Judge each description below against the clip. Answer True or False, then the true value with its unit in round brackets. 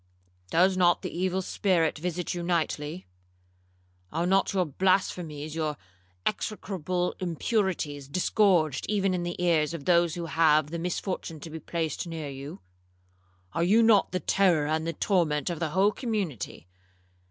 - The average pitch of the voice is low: False (170 Hz)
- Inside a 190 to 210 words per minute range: False (150 wpm)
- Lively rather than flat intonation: False (3.0 semitones)